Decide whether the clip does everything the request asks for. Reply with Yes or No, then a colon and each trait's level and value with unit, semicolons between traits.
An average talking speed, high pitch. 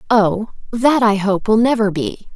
Yes: average, 180 wpm; high, 215 Hz